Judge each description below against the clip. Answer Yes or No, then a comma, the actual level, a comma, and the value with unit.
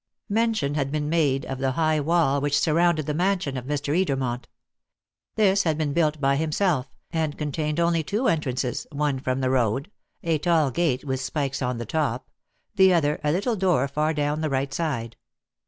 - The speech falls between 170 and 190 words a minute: Yes, average, 185 wpm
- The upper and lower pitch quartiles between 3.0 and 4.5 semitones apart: Yes, average, 3.5 semitones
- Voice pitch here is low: No, medium, 150 Hz